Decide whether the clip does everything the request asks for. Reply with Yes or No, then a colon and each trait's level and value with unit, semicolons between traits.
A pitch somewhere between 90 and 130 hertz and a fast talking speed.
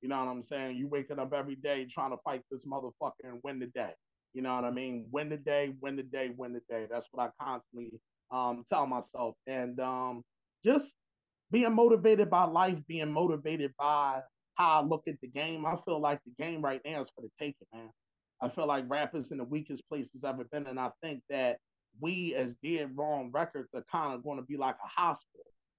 No: medium, 140 Hz; fast, 225 wpm